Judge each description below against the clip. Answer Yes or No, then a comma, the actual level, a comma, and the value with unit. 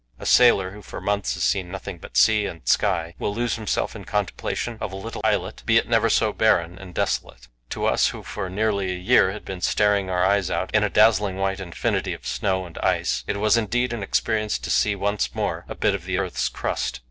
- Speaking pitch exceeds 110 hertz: No, low, 100 Hz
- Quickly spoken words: Yes, fast, 230 wpm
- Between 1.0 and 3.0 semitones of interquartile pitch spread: Yes, narrow, 2.4 semitones